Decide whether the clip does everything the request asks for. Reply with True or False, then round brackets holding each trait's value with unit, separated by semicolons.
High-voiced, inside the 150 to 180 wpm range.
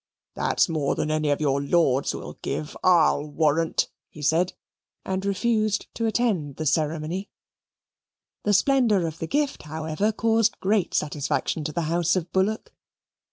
False (165 Hz; 155 wpm)